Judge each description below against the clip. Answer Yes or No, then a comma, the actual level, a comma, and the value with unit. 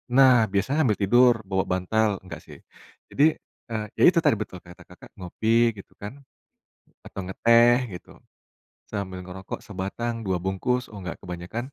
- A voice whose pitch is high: No, low, 100 Hz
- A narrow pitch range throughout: No, average, 4.1 semitones